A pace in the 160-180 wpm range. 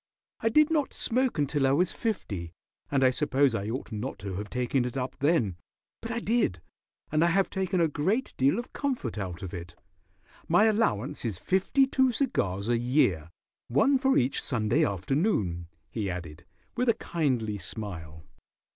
Yes: average, 175 wpm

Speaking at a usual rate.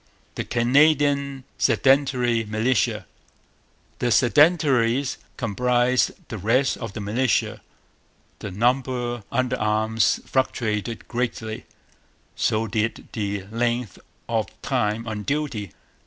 No: slow, 95 wpm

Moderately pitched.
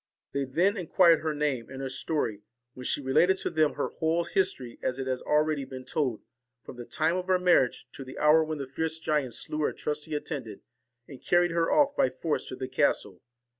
Yes: medium, 150 Hz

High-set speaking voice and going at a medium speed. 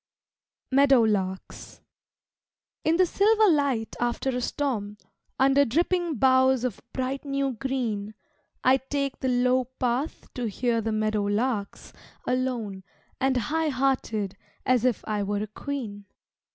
No: very high, 255 Hz; slow, 125 wpm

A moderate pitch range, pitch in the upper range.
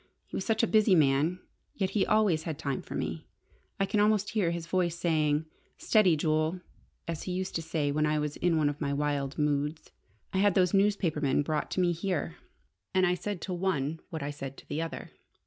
No: average, 4.0 semitones; medium, 165 Hz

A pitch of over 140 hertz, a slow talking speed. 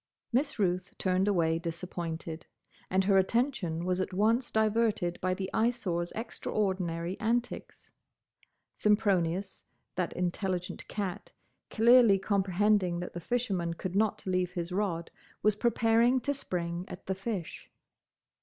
Yes: high, 190 Hz; slow, 125 wpm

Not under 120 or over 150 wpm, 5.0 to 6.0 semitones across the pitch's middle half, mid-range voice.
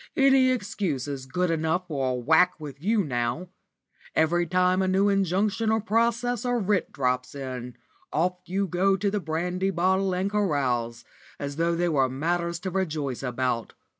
No: average, 165 wpm; wide, 5.6 semitones; medium, 175 Hz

